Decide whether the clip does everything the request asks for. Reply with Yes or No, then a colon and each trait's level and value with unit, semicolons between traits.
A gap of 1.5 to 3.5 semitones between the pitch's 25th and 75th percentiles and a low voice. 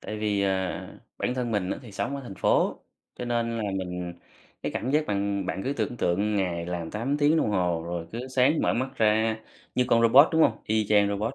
No: average, 4.4 semitones; low, 105 Hz